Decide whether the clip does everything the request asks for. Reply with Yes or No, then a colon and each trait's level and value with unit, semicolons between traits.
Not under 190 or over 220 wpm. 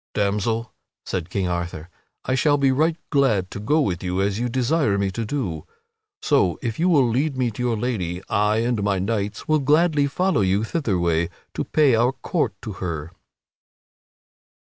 No: average, 175 wpm